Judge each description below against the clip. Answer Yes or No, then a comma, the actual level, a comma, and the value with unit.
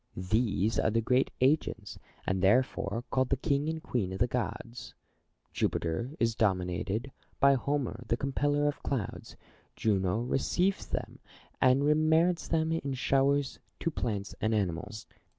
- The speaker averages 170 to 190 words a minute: No, average, 140 wpm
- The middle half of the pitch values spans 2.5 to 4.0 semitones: No, average, 5.0 semitones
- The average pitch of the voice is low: Yes, low, 125 Hz